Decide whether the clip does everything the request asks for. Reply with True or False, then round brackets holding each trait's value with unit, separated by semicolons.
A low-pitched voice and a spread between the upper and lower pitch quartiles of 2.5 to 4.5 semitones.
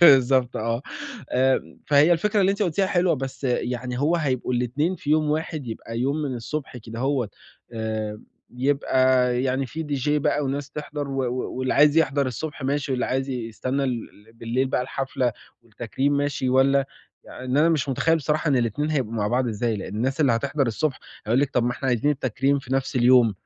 True (130 Hz; 2.9 semitones)